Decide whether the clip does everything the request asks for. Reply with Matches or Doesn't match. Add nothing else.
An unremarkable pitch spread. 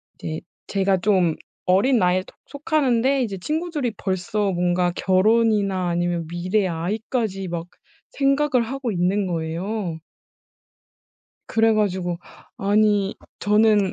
Matches